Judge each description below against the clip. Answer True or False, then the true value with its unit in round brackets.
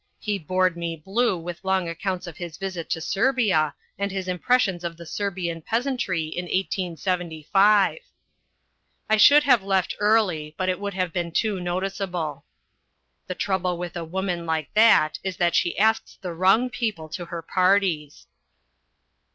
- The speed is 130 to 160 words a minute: True (155 wpm)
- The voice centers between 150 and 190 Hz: True (185 Hz)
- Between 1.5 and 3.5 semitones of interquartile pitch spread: True (2.8 semitones)